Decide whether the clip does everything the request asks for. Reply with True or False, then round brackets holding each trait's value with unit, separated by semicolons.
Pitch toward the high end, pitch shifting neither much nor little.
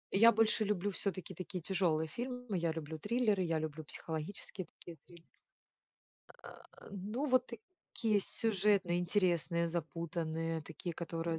False (175 Hz; 4.0 semitones)